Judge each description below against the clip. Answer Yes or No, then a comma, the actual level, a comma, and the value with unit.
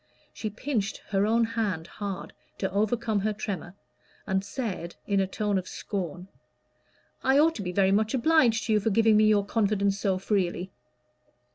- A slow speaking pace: No, average, 170 wpm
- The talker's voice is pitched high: Yes, high, 205 Hz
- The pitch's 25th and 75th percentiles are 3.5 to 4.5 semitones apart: No, narrow, 2.5 semitones